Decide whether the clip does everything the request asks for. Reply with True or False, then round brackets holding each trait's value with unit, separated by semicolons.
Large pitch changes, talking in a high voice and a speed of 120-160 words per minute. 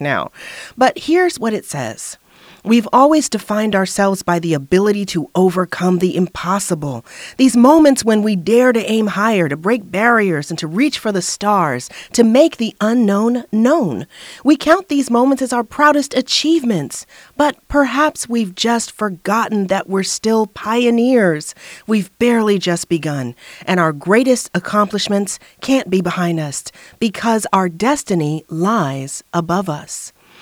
False (4.9 semitones; 215 Hz; 145 wpm)